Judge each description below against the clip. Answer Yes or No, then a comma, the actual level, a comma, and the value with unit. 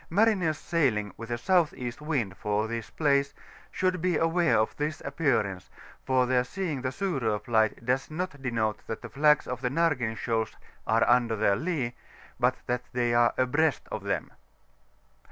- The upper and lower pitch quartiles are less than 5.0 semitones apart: No, average, 5.3 semitones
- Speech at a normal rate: Yes, average, 165 wpm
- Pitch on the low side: Yes, low, 130 Hz